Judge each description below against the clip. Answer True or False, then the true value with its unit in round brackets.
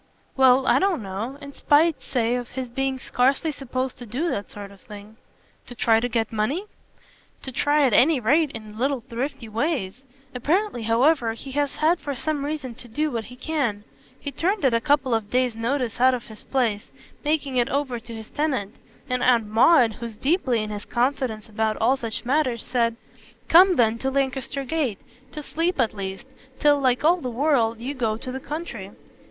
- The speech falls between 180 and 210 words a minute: True (195 wpm)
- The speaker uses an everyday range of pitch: True (4.1 semitones)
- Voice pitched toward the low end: False (255 Hz)